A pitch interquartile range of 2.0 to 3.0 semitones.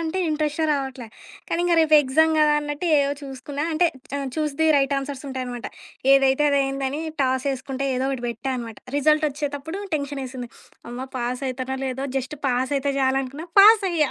Yes: narrow, 2.4 semitones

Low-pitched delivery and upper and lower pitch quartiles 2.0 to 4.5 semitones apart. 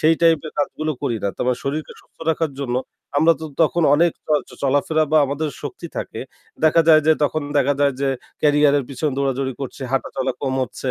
No: medium, 145 Hz; narrow, 2.5 semitones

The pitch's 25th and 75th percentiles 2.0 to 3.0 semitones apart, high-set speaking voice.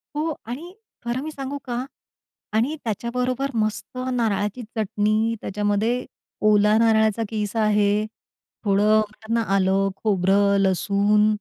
Yes: narrow, 2.6 semitones; high, 215 Hz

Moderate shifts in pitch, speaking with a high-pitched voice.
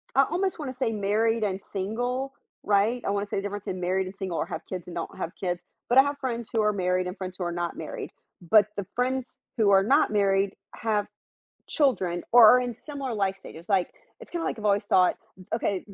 Yes: average, 4.5 semitones; high, 205 Hz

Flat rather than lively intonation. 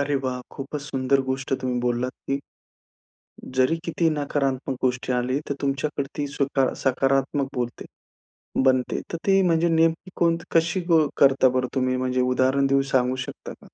Yes: narrow, 2.2 semitones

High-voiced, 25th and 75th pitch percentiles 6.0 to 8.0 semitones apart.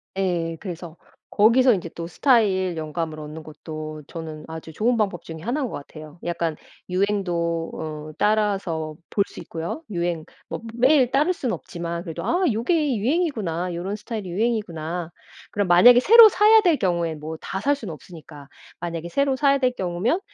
No: medium, 180 Hz; wide, 6.5 semitones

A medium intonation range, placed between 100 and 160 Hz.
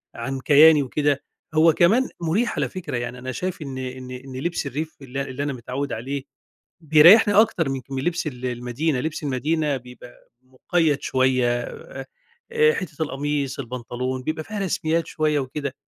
Yes: average, 3.6 semitones; medium, 140 Hz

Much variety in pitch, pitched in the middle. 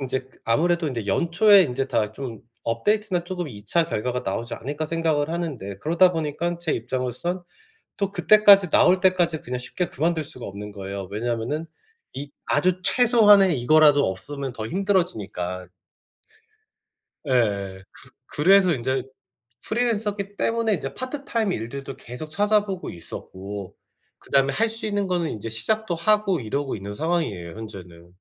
Yes: wide, 8.3 semitones; medium, 155 Hz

